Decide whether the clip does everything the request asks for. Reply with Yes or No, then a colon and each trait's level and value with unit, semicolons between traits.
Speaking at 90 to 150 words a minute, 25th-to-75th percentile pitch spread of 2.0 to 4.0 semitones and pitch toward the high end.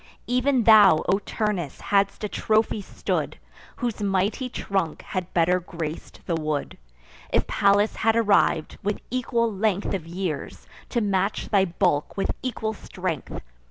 Yes: average, 140 wpm; average, 3.4 semitones; high, 200 Hz